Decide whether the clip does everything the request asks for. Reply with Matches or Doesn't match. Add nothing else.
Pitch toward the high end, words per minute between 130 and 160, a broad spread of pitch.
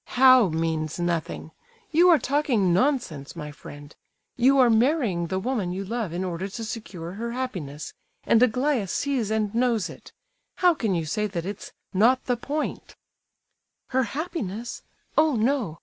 Matches